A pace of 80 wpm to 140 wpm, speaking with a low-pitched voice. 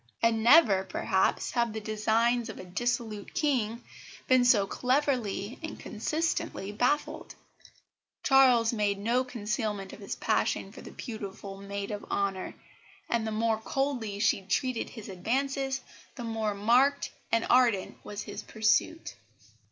No: slow, 135 wpm; high, 225 Hz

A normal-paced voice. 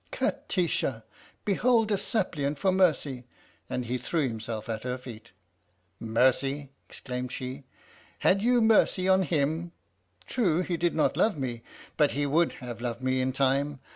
Yes: average, 170 wpm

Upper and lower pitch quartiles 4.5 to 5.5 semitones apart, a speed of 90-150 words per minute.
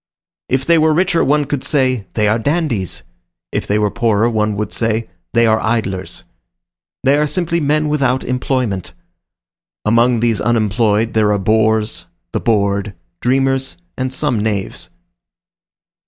No: average, 4.0 semitones; average, 140 wpm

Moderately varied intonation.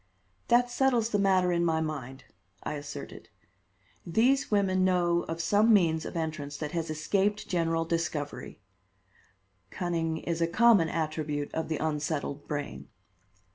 Yes: average, 3.4 semitones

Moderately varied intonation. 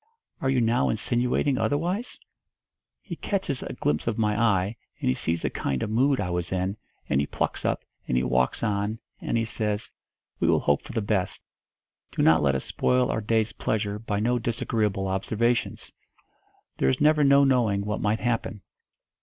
Yes: average, 4.2 semitones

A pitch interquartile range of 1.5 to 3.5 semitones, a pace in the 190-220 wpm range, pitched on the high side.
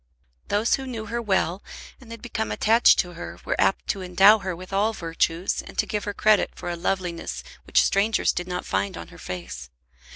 No: average, 4.0 semitones; fast, 205 wpm; high, 195 Hz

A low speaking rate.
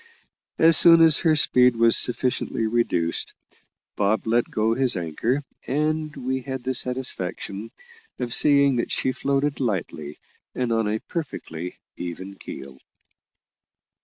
Yes: slow, 130 wpm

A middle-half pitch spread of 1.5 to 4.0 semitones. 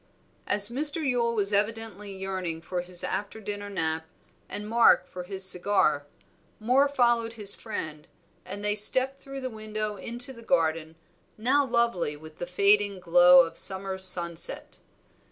No: average, 4.4 semitones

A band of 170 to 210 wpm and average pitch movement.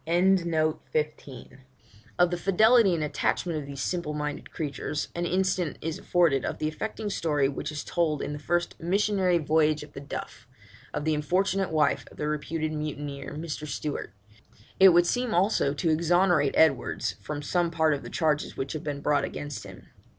Yes: average, 175 wpm; average, 3.0 semitones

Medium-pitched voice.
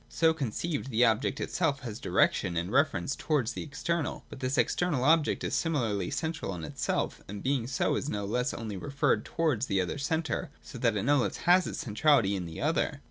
No: low, 130 Hz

